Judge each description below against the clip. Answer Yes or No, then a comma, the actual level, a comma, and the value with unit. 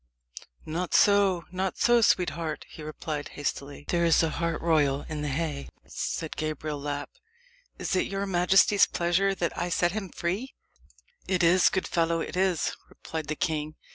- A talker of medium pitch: Yes, medium, 170 Hz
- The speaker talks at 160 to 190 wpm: Yes, average, 165 wpm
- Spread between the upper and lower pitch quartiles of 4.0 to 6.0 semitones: No, average, 3.2 semitones